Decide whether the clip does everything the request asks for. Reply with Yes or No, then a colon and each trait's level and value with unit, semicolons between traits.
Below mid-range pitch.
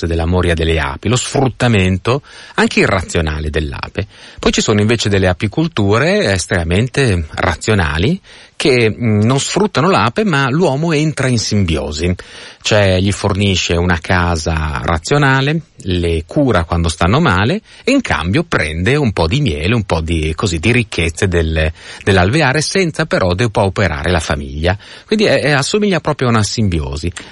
Yes: low, 100 Hz